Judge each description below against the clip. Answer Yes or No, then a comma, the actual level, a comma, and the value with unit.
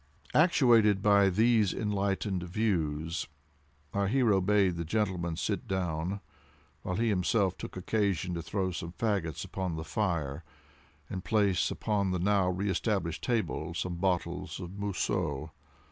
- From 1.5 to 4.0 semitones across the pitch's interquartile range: Yes, average, 3.1 semitones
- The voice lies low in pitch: Yes, very low, 95 Hz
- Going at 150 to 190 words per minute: No, slow, 135 wpm